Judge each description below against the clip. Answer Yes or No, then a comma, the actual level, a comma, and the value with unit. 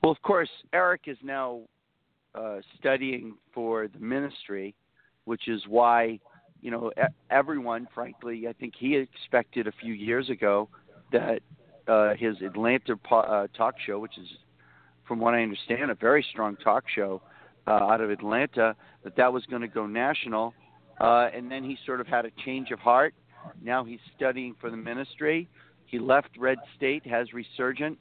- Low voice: Yes, low, 120 Hz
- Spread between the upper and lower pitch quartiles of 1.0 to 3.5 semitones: Yes, average, 2.7 semitones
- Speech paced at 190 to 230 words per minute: No, average, 165 wpm